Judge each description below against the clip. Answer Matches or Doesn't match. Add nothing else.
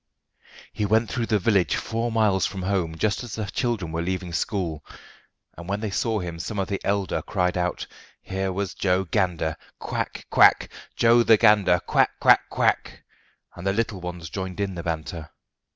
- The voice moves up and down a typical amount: Matches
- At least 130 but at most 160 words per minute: Doesn't match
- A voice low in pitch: Matches